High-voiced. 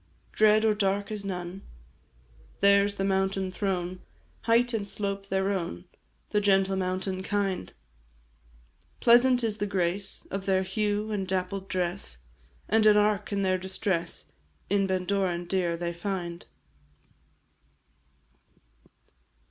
Yes: high, 195 Hz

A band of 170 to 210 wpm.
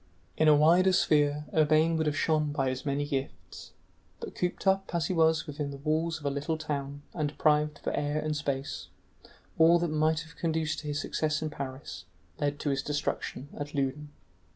Yes: average, 195 wpm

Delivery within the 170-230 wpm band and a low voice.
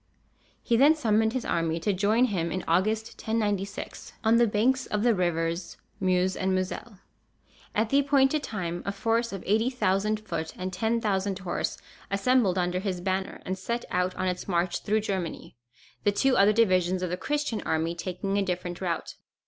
No: average, 175 wpm; high, 195 Hz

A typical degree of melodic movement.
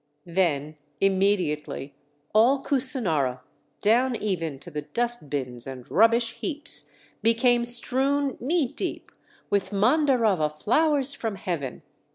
No: wide, 8.5 semitones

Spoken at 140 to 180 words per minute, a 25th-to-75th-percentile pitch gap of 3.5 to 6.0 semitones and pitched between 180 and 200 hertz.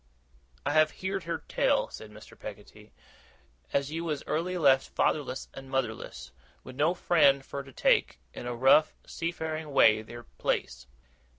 No: average, 155 wpm; average, 4.5 semitones; medium, 140 Hz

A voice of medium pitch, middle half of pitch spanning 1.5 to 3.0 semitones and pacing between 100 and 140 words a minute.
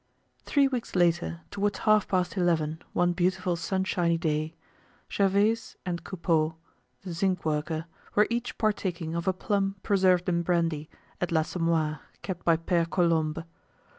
Yes: medium, 175 Hz; narrow, 2.6 semitones; slow, 135 wpm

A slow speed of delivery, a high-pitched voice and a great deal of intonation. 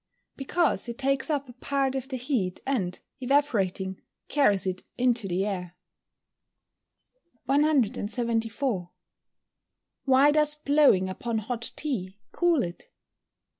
Yes: slow, 115 wpm; high, 245 Hz; wide, 6.2 semitones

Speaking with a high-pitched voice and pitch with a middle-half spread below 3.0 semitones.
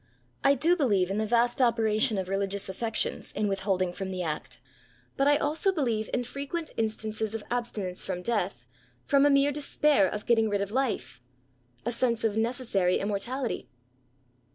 No: high, 220 Hz; average, 4.7 semitones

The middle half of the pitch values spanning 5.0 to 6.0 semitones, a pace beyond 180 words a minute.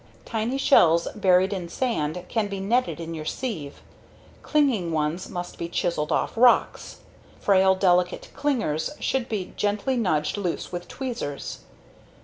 No: wide, 5.4 semitones; slow, 135 wpm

